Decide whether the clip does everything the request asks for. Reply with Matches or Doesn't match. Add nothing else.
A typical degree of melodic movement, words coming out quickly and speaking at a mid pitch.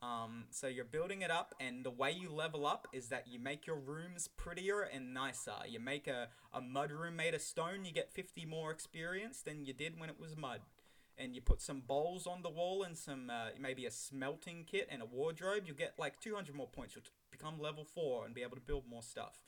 Matches